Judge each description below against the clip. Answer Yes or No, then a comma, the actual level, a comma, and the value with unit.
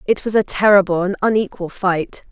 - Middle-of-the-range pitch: No, high, 195 Hz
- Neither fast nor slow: Yes, average, 180 wpm